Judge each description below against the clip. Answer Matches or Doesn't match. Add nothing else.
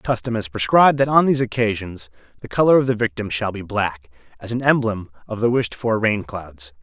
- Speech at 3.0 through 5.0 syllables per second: Doesn't match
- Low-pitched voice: Matches